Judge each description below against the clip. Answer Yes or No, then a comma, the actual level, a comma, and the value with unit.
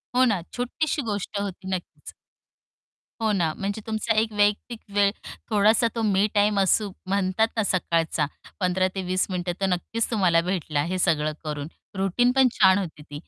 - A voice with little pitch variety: No, average, 3.3 semitones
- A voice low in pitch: No, high, 195 Hz